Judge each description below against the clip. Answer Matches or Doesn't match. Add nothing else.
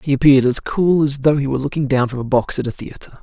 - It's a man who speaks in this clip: Matches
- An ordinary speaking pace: Doesn't match